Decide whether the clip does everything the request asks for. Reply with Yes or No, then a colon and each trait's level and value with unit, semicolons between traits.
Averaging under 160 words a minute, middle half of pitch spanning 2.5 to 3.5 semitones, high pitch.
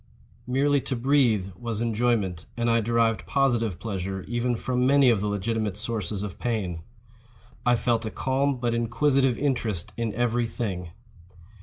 No: average, 150 wpm; average, 3.0 semitones; low, 115 Hz